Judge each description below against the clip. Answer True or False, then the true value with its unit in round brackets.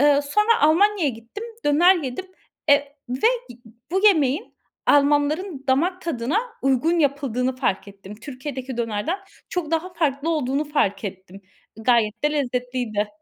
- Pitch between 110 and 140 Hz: False (280 Hz)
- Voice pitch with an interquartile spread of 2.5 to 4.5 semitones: False (4.9 semitones)